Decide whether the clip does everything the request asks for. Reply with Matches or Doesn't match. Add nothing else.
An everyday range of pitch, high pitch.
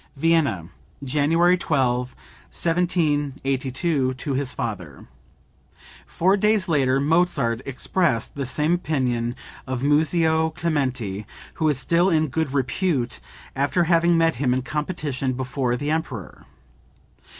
Doesn't match